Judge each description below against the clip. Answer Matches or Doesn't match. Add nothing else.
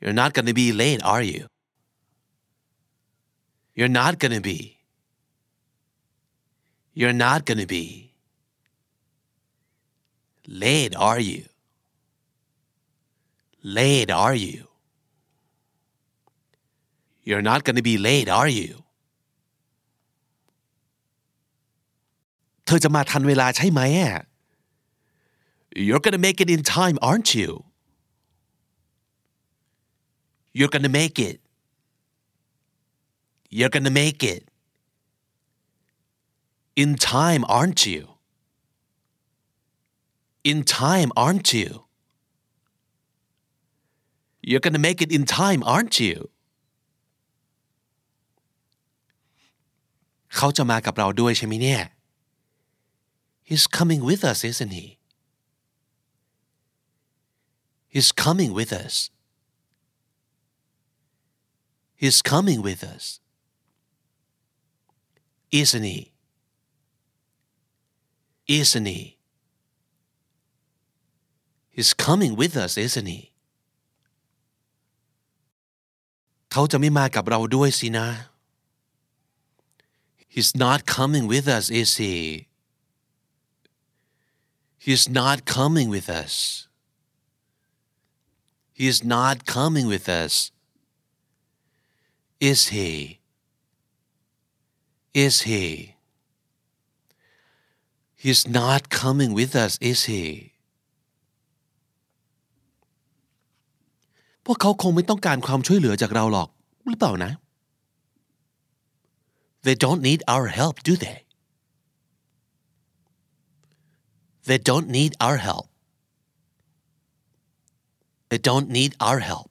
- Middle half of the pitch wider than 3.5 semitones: Doesn't match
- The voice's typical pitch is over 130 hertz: Matches